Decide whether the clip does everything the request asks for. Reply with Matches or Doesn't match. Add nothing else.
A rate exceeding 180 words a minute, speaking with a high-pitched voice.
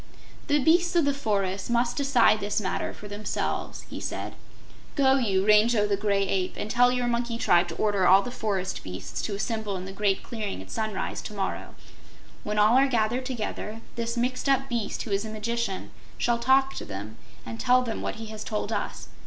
Matches